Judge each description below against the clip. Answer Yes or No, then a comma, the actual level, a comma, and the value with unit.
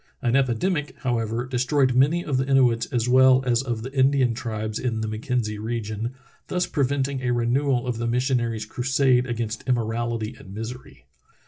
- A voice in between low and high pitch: No, low, 125 Hz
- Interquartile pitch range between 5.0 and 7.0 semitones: No, narrow, 2.4 semitones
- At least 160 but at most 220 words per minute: Yes, average, 165 wpm